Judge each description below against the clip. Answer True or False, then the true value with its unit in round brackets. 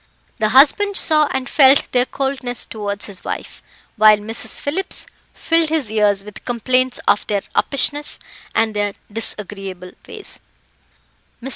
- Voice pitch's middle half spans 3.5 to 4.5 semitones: False (5.1 semitones)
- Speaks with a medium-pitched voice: False (245 Hz)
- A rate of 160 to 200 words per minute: False (135 wpm)